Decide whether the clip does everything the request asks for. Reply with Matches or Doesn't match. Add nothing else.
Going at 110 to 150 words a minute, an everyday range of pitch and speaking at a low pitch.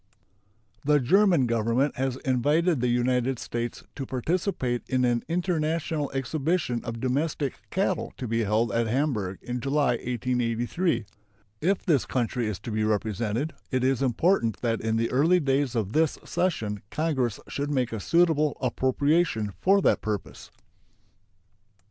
Matches